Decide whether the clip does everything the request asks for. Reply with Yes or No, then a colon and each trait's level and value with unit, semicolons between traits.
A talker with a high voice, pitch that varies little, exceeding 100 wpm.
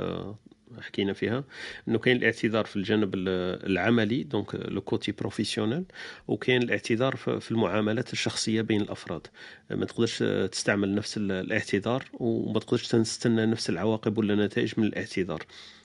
No: low, 110 Hz; narrow, 1.9 semitones; average, 120 wpm